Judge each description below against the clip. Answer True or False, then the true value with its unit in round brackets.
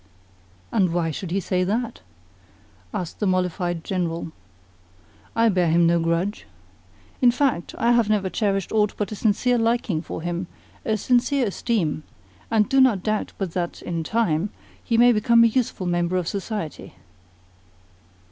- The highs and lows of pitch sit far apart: False (4.8 semitones)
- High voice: True (195 Hz)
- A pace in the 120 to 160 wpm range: True (155 wpm)